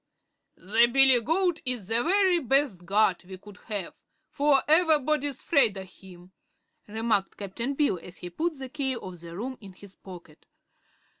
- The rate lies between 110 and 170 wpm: Yes, average, 155 wpm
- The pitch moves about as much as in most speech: No, wide, 6.9 semitones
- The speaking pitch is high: Yes, high, 235 Hz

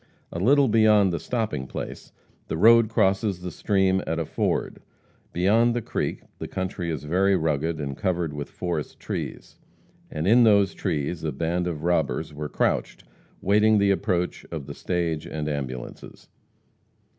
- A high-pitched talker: No, very low, 90 Hz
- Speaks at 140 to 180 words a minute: Yes, average, 155 wpm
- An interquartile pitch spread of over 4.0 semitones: Yes, average, 4.4 semitones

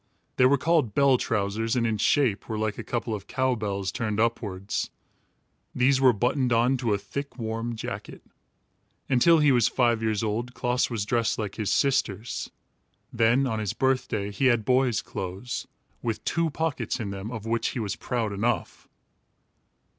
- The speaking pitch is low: Yes, low, 115 Hz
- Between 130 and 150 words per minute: No, average, 170 wpm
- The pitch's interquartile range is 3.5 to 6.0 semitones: No, average, 3.1 semitones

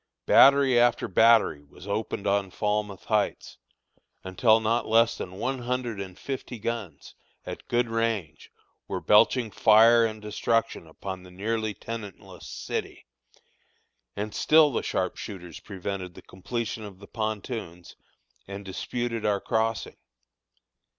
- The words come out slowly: Yes, slow, 125 wpm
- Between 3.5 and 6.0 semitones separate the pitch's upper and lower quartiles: No, average, 2.9 semitones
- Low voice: Yes, low, 110 Hz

